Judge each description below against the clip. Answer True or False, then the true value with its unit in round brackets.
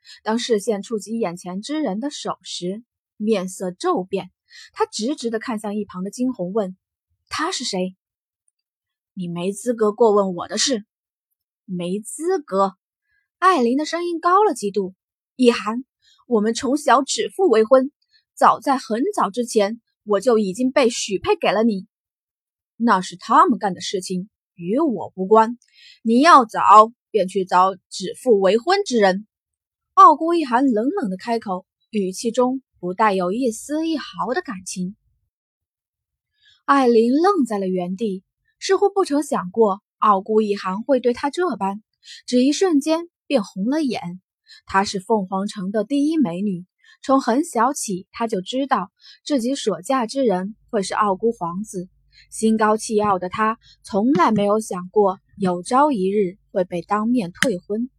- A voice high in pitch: True (220 Hz)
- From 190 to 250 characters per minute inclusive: True (215 characters per minute)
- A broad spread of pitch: True (5.8 semitones)